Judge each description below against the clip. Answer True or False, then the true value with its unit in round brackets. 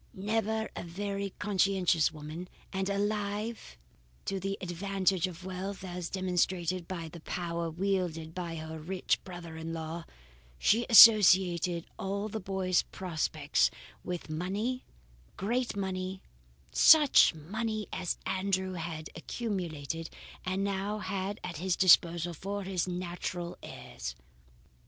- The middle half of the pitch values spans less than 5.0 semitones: True (2.7 semitones)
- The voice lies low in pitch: False (185 Hz)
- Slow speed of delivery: True (120 wpm)